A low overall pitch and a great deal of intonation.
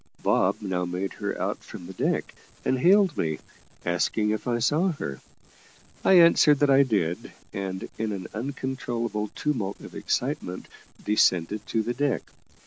Yes: low, 110 Hz; wide, 6.6 semitones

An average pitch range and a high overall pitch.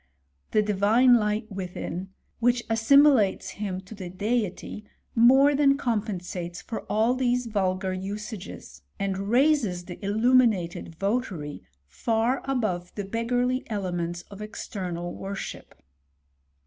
Yes: average, 4.5 semitones; high, 210 Hz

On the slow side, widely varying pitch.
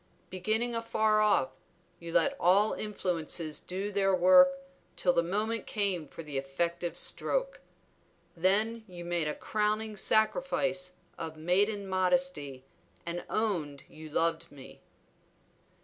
No: slow, 120 wpm; average, 4.3 semitones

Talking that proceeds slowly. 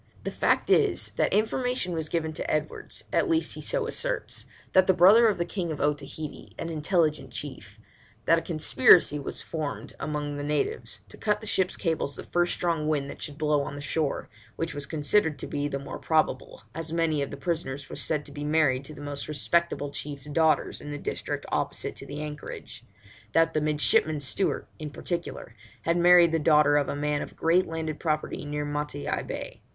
No: average, 200 wpm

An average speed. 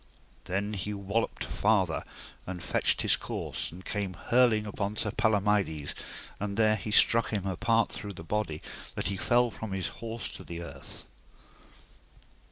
Yes: average, 160 wpm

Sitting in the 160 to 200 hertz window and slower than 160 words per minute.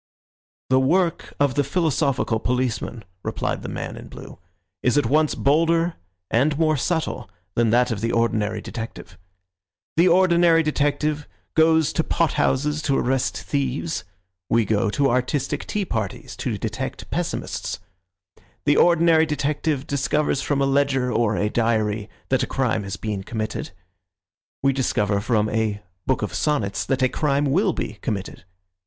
No: low, 135 Hz; average, 150 wpm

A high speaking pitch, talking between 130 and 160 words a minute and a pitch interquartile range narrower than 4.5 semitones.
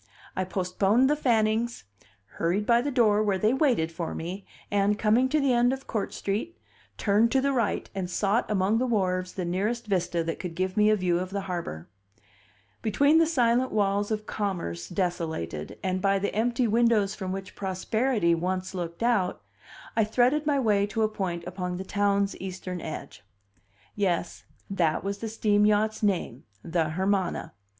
No: high, 200 Hz; average, 175 wpm; average, 3.7 semitones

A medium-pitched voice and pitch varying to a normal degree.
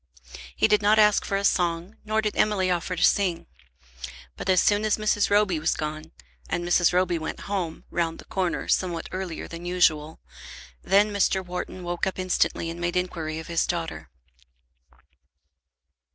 Yes: medium, 180 Hz; average, 3.0 semitones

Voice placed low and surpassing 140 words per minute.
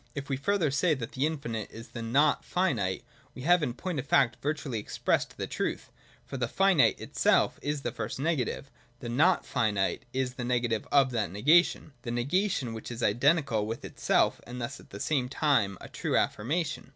Yes: low, 130 Hz; average, 195 wpm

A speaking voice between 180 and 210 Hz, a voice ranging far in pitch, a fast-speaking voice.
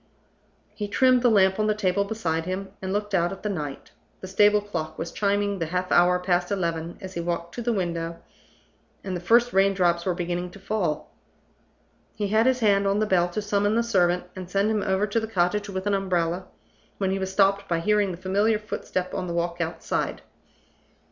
No: high, 190 Hz; average, 2.8 semitones; fast, 210 wpm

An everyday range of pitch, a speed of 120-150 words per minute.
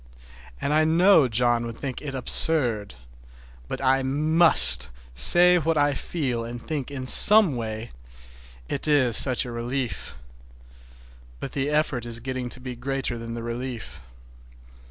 Yes: average, 3.9 semitones; average, 140 wpm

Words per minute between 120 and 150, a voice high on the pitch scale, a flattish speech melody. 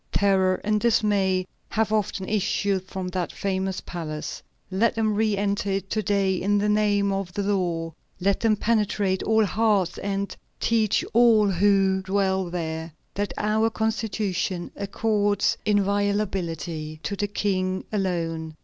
Yes: average, 140 wpm; high, 200 Hz; narrow, 2.0 semitones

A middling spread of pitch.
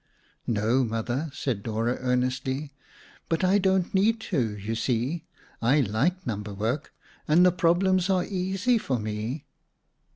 No: wide, 8.1 semitones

